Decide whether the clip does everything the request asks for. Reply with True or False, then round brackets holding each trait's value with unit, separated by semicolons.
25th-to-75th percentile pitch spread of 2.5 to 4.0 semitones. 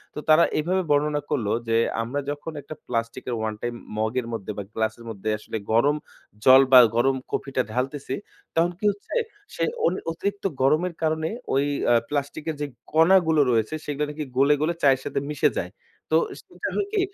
False (4.8 semitones)